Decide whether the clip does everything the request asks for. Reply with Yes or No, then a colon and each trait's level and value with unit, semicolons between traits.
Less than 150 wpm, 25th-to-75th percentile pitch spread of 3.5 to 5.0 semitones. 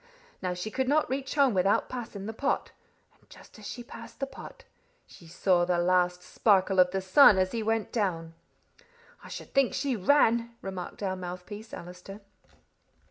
No: average, 175 wpm; average, 4.6 semitones